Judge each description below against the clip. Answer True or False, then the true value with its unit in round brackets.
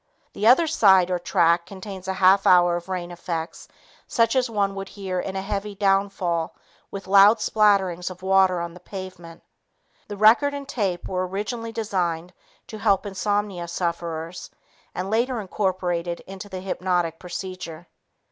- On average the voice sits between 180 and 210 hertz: True (190 Hz)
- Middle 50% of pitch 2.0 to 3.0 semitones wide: True (2.5 semitones)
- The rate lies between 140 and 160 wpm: True (155 wpm)